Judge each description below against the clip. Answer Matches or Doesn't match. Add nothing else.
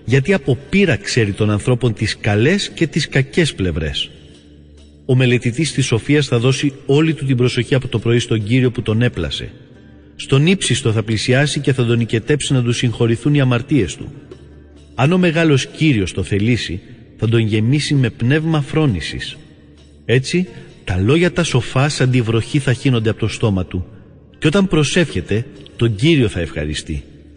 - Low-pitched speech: Matches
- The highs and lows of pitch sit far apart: Matches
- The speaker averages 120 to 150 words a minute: Doesn't match